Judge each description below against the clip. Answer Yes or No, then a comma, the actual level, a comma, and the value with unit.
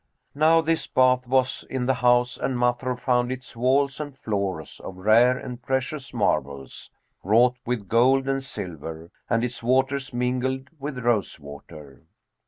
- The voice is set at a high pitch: No, low, 125 Hz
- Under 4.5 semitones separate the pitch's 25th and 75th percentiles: Yes, average, 3.4 semitones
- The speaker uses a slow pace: No, average, 150 wpm